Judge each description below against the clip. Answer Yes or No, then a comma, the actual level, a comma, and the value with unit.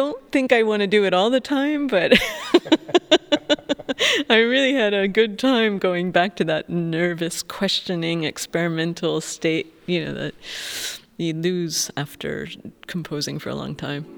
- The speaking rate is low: No, average, 155 wpm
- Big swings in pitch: Yes, wide, 7.7 semitones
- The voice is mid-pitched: No, high, 195 Hz